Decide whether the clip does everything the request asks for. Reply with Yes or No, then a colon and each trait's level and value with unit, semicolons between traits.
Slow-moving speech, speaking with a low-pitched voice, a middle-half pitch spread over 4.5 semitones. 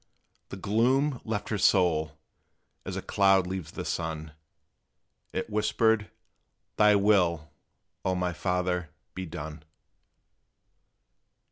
No: slow, 105 wpm; very low, 95 Hz; average, 3.8 semitones